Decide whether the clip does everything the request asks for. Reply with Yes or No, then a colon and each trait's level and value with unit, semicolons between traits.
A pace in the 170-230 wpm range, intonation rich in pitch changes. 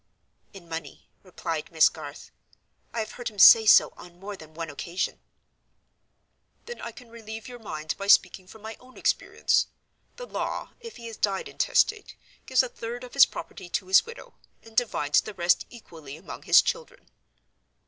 Yes: average, 175 wpm; wide, 6.1 semitones